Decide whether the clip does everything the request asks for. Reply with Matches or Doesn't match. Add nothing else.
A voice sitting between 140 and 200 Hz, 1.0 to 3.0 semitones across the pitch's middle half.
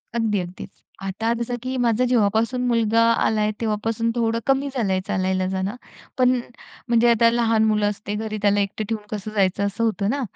Doesn't match